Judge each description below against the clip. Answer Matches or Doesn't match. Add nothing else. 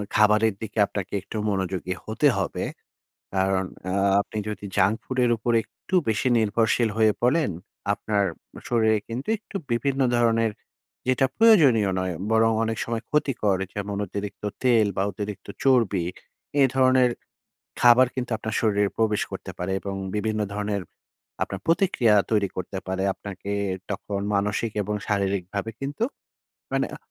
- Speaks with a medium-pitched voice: Doesn't match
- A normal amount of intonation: Matches